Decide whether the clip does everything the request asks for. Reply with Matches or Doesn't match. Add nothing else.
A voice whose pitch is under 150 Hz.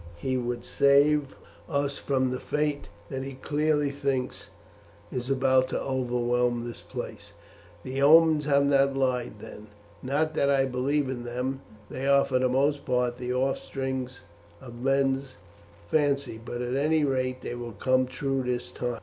Matches